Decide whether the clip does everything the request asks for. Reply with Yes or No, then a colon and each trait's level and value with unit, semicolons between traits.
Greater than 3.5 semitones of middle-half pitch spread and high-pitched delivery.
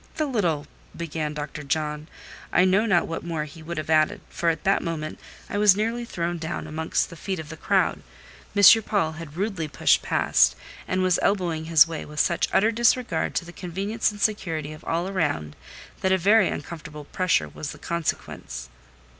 No: average, 3.9 semitones; medium, 170 Hz